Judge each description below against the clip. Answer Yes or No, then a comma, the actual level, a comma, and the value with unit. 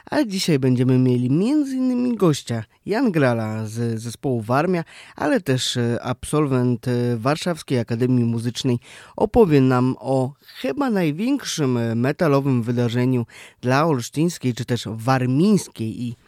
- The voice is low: Yes, low, 130 Hz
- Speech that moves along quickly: No, average, 115 wpm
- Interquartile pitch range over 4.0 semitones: Yes, average, 4.7 semitones